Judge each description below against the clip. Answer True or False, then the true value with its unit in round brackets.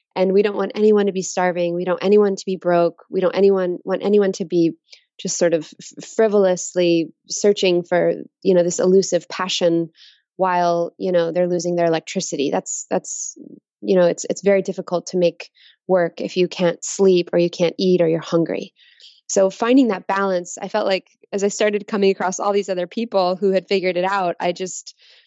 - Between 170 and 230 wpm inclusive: True (200 wpm)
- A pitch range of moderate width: False (2.0 semitones)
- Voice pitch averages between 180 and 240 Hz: True (185 Hz)